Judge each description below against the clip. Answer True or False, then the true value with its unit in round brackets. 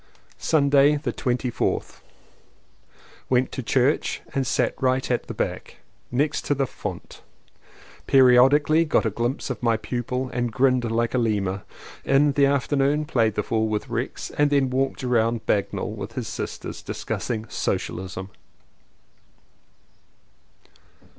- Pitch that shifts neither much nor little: True (3.1 semitones)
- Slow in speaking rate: True (130 wpm)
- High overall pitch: False (125 Hz)